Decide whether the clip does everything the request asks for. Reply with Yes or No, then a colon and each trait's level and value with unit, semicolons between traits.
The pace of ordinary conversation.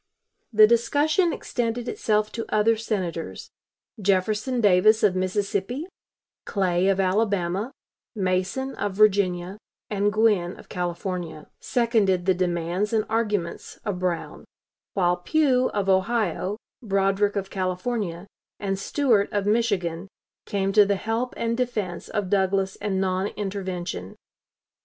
No: slow, 120 wpm